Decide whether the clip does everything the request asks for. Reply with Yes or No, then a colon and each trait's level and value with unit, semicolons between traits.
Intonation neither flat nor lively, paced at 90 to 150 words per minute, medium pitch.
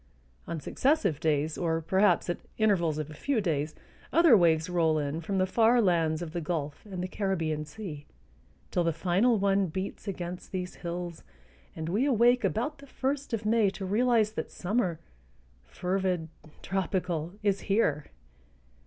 No: average, 4.6 semitones; average, 160 wpm; medium, 180 Hz